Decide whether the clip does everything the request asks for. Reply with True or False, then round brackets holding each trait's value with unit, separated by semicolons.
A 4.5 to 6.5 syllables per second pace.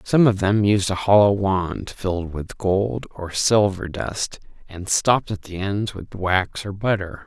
False (4.0 syllables/s)